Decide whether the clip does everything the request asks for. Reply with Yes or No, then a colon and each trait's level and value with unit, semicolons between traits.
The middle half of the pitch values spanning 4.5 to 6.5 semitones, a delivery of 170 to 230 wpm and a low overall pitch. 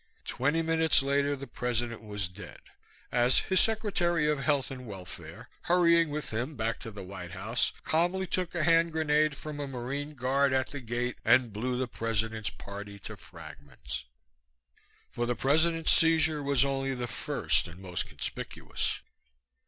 No: wide, 5.4 semitones; average, 160 wpm; low, 130 Hz